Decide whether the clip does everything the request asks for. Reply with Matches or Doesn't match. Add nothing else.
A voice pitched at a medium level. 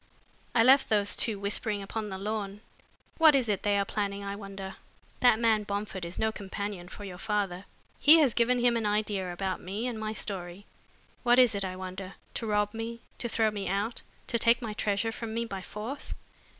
Doesn't match